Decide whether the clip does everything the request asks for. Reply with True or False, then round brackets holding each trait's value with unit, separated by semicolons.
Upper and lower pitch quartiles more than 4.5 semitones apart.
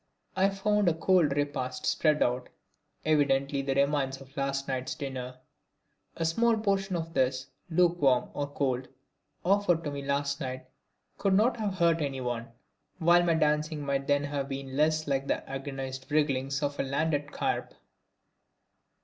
False (3.4 semitones)